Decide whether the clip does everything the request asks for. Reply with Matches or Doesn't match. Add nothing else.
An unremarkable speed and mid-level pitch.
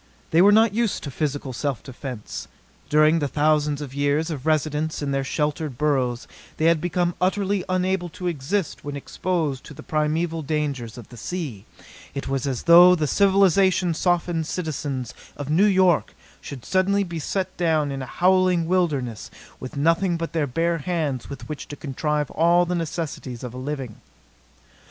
Matches